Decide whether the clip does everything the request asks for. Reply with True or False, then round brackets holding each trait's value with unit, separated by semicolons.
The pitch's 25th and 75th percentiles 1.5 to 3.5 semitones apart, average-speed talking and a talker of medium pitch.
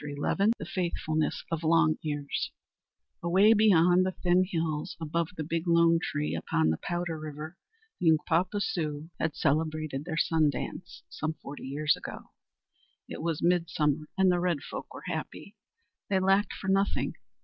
True (2.7 semitones; 155 wpm; 165 Hz)